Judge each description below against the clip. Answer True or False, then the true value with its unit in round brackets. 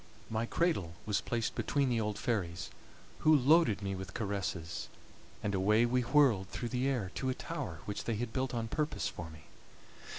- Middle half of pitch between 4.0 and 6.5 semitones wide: True (5.0 semitones)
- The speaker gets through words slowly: False (185 wpm)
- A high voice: False (115 Hz)